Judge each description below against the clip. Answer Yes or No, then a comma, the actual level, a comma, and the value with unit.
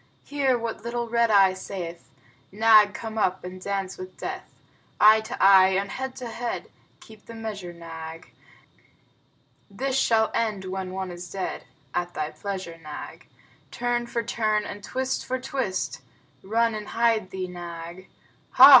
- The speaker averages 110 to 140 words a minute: No, average, 155 wpm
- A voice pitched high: Yes, high, 205 Hz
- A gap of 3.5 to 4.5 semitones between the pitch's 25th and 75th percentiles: Yes, average, 3.9 semitones